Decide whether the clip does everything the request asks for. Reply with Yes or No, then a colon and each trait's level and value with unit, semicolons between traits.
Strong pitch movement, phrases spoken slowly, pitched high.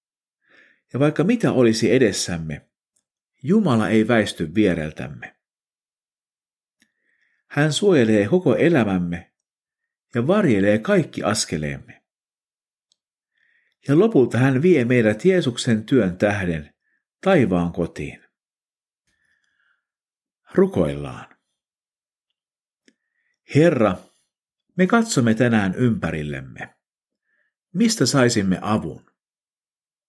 No: wide, 8.8 semitones; slow, 70 wpm; low, 115 Hz